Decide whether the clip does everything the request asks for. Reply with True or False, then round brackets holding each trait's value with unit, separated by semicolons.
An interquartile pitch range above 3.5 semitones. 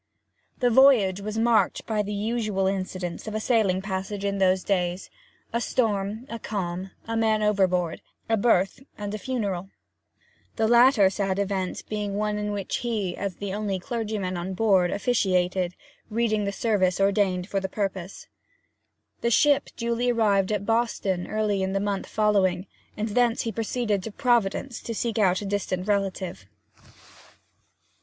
False (2.8 semitones)